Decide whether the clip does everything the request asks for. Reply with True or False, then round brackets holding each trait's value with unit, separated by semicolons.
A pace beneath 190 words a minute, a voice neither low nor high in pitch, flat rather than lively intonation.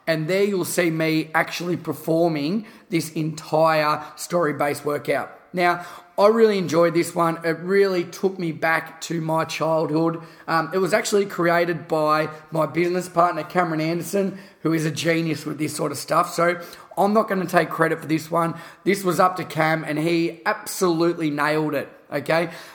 True (170 wpm; 165 Hz; 1.8 semitones)